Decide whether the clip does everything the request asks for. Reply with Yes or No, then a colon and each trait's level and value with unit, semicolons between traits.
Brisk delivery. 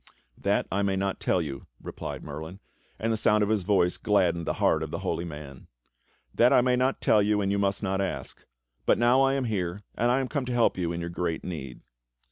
Yes: fast, 240 wpm